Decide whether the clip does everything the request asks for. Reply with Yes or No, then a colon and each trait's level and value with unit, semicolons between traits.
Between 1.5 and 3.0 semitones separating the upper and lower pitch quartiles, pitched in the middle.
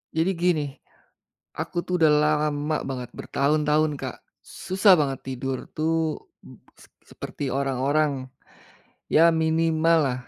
Yes: average, 2.7 semitones; medium, 155 Hz